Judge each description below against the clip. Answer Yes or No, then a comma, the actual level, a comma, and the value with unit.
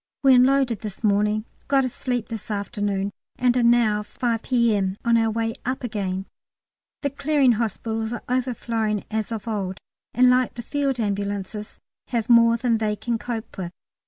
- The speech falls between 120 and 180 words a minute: Yes, average, 165 wpm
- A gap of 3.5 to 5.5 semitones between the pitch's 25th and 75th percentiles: No, average, 2.8 semitones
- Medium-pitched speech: No, high, 225 Hz